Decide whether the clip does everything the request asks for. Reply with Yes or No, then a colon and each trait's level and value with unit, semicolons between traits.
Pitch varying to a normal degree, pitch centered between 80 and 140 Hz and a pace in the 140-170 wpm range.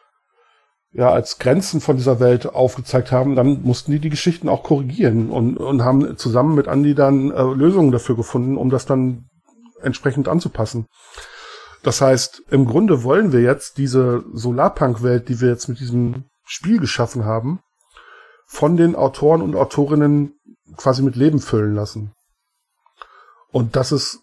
Yes: average, 3.0 semitones; low, 135 Hz; average, 150 wpm